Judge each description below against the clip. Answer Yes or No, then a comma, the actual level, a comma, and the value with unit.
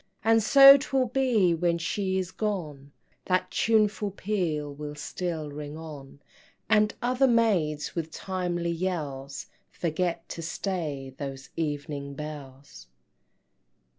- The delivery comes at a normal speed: No, slow, 115 wpm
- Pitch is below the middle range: No, medium, 170 Hz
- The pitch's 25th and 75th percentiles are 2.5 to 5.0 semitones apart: No, wide, 5.5 semitones